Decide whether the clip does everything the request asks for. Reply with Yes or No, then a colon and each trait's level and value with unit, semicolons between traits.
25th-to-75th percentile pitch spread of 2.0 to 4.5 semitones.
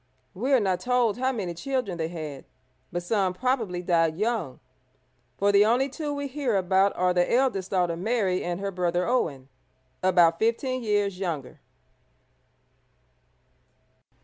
No: wide, 5.5 semitones